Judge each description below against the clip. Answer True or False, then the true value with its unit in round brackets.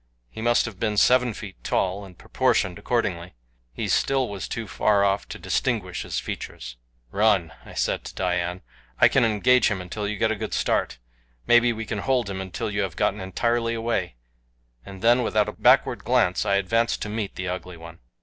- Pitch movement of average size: True (3.7 semitones)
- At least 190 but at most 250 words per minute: True (195 wpm)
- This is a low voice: True (105 Hz)